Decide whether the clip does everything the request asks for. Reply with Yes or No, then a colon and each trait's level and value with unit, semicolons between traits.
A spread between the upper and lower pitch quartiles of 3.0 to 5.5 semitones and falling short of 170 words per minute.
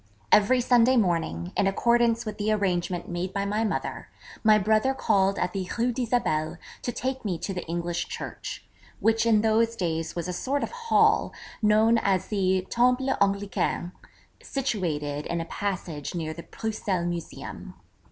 Yes: average, 4.7 semitones; average, 160 wpm